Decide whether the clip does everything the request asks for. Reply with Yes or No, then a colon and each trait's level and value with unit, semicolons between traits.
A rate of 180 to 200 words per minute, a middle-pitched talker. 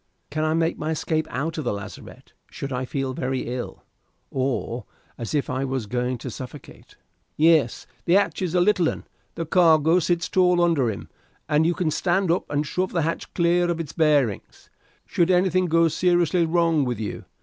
Yes: average, 190 wpm; medium, 160 Hz